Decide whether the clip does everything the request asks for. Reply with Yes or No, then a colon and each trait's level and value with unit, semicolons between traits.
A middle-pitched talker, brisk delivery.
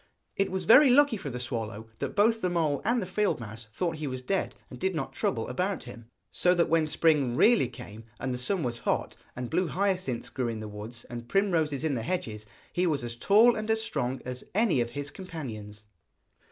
Yes: medium, 145 Hz; fast, 220 wpm